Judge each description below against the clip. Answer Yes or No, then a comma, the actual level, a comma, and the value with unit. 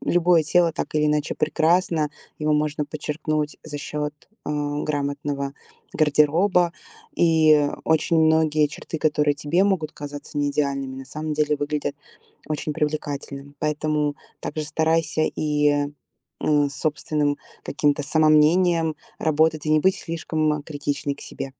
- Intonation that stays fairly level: Yes, narrow, 1.3 semitones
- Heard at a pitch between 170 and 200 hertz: No, medium, 150 Hz